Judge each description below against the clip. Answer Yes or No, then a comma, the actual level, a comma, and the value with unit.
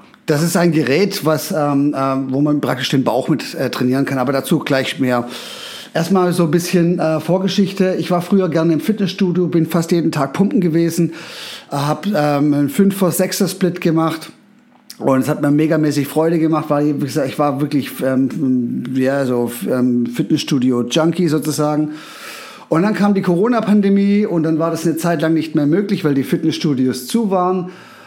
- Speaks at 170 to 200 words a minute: Yes, average, 185 wpm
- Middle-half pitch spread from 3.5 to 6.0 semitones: Yes, average, 4.0 semitones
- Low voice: No, medium, 160 Hz